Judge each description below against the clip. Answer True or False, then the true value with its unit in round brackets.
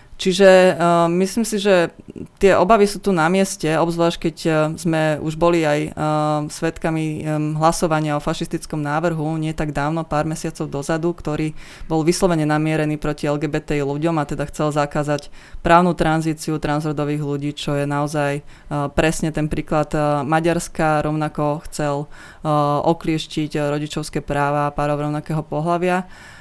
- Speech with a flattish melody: True (2.1 semitones)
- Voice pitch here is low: False (155 Hz)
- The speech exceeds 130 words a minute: True (150 wpm)